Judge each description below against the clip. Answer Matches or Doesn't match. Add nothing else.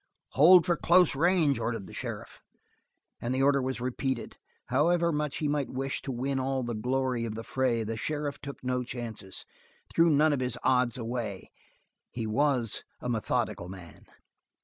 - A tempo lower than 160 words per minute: Doesn't match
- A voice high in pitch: Doesn't match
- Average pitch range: Matches